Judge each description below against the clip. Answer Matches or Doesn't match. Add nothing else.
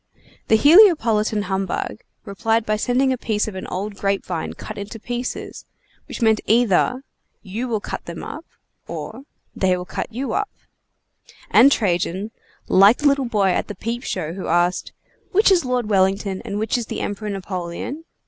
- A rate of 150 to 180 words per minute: Matches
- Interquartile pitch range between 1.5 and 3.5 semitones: Doesn't match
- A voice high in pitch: Matches